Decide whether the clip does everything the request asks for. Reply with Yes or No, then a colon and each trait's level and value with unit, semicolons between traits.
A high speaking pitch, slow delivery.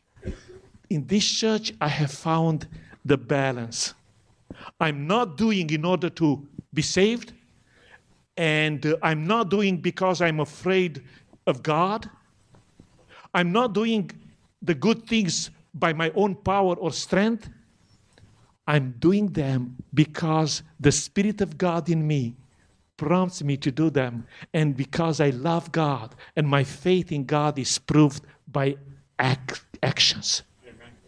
No: medium, 155 Hz; slow, 130 wpm